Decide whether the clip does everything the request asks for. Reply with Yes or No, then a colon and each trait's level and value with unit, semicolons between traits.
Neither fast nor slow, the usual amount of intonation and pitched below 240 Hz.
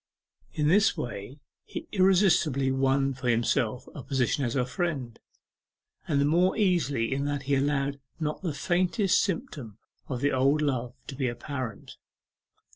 Yes: average, 150 wpm; average, 3.7 semitones; medium, 140 Hz